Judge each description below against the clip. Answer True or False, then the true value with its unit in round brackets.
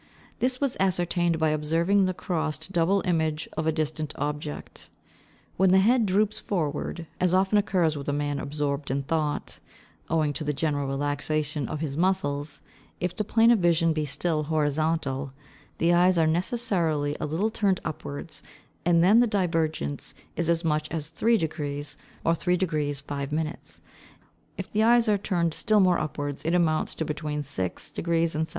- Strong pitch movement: False (3.5 semitones)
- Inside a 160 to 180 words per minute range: True (165 wpm)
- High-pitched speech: False (160 Hz)